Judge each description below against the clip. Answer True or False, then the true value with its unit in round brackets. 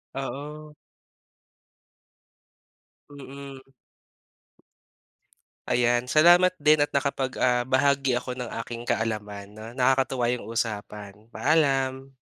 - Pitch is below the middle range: True (130 Hz)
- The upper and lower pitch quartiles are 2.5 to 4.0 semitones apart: True (2.9 semitones)